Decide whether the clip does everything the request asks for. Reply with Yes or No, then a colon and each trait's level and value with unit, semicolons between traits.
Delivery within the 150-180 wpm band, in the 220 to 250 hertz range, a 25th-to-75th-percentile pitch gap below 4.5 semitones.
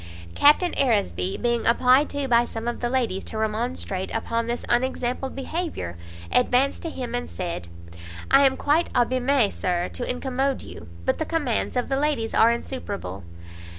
Yes: average, 160 wpm; high, 245 Hz; average, 3.2 semitones